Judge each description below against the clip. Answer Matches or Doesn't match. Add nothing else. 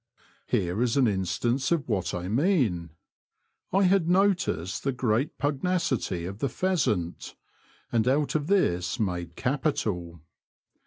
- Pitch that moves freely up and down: Matches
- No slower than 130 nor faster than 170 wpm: Matches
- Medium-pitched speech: Doesn't match